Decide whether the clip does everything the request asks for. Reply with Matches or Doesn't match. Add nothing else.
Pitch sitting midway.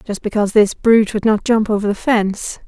Doesn't match